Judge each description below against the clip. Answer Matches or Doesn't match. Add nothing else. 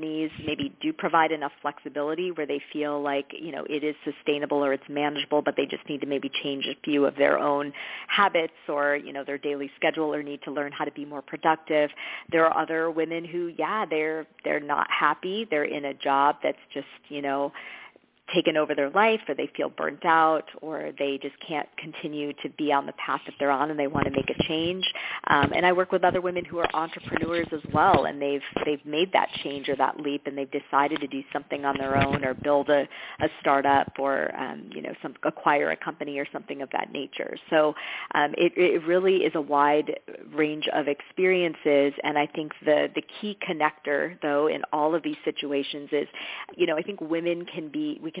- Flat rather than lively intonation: Matches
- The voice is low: Doesn't match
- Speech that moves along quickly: Matches